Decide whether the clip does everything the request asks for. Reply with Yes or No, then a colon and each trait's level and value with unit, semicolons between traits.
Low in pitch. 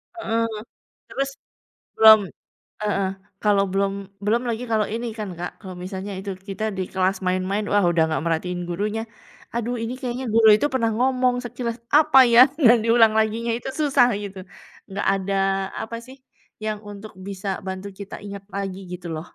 No: high, 210 Hz